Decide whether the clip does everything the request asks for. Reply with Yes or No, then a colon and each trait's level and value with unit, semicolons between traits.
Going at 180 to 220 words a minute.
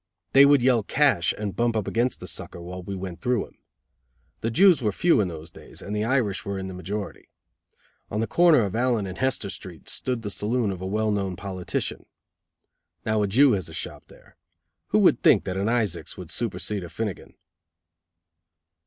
Yes: average, 195 wpm